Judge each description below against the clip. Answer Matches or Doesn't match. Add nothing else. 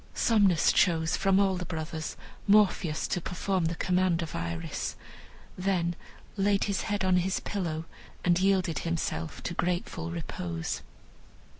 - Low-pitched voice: Doesn't match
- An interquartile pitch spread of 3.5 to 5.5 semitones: Doesn't match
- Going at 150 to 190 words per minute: Doesn't match